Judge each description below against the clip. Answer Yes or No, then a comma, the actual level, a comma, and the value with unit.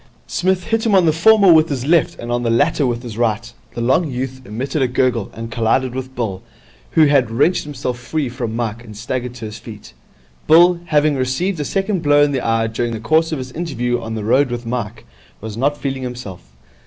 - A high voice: No, low, 125 Hz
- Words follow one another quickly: Yes, fast, 220 wpm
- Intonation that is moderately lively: Yes, average, 4.6 semitones